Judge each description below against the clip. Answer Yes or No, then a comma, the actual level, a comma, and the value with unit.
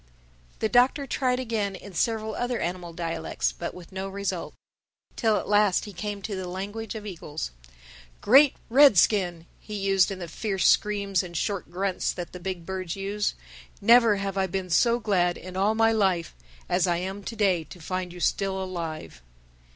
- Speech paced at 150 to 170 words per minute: No, average, 180 wpm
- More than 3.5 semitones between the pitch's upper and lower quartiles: No, average, 2.9 semitones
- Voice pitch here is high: Yes, high, 195 Hz